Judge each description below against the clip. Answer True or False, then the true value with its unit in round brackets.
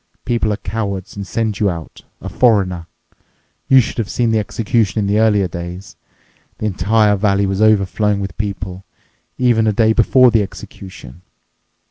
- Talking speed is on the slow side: False (150 wpm)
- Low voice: True (105 Hz)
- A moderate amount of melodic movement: False (2.3 semitones)